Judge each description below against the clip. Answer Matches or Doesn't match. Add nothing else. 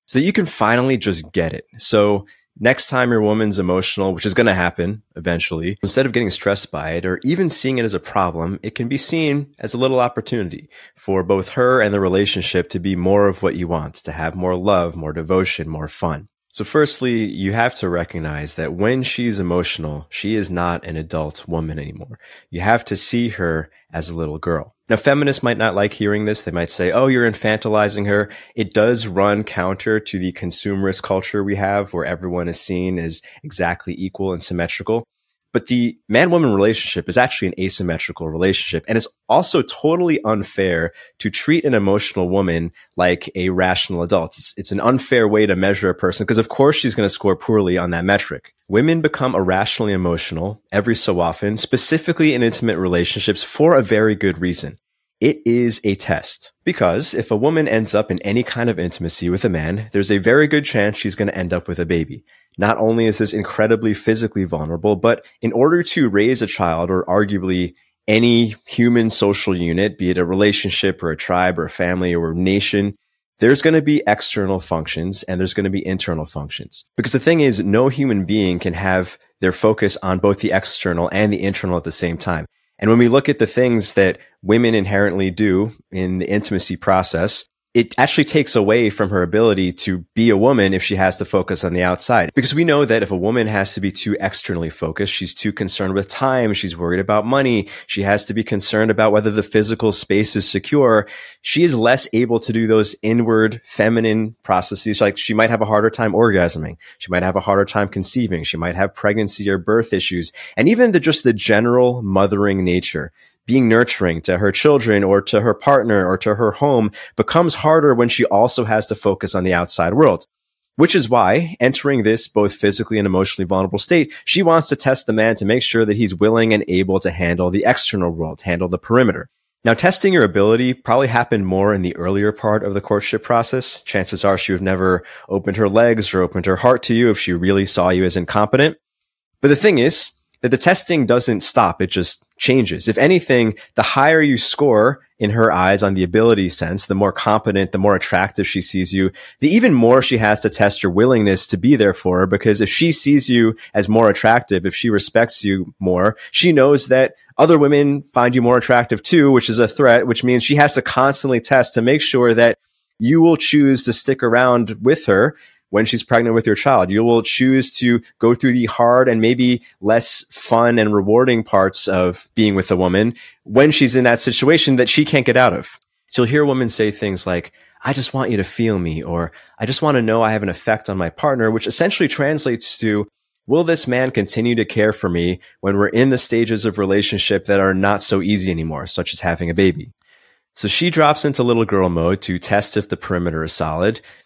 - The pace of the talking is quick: Matches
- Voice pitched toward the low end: Matches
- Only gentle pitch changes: Doesn't match